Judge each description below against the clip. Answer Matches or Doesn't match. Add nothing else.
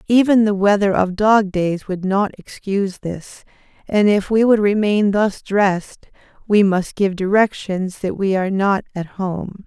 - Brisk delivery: Doesn't match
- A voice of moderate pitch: Doesn't match